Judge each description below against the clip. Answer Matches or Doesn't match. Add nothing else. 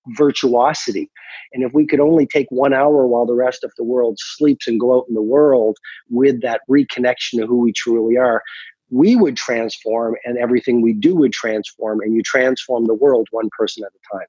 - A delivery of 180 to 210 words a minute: Matches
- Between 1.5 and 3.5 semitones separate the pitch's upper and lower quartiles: Matches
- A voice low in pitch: Matches